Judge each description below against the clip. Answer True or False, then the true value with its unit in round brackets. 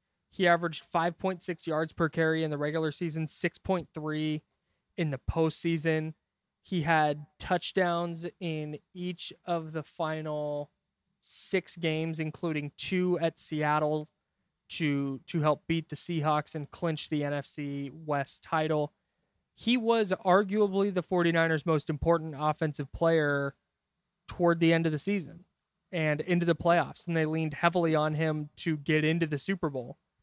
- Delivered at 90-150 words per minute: True (140 wpm)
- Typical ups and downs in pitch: False (2.2 semitones)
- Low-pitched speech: False (160 Hz)